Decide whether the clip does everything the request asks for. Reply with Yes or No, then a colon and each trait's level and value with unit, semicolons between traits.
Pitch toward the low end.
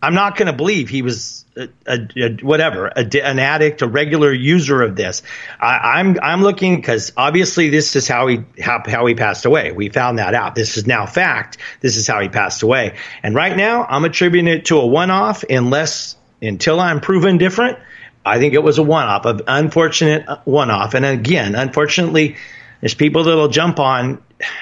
No: medium, 150 Hz